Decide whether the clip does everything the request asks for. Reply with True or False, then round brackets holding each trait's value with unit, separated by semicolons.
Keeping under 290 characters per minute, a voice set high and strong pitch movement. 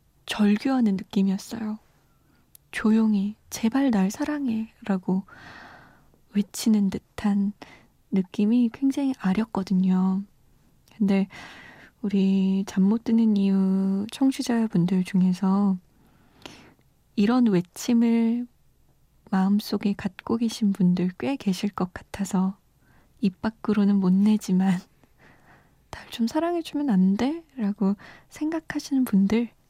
False (210 characters per minute; 205 Hz; 3.1 semitones)